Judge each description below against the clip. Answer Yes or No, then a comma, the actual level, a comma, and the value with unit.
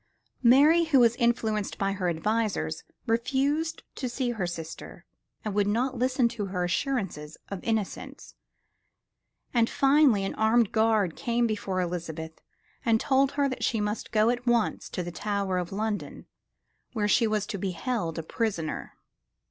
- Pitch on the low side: No, high, 220 Hz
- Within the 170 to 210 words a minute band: No, average, 155 wpm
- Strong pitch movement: No, average, 4.1 semitones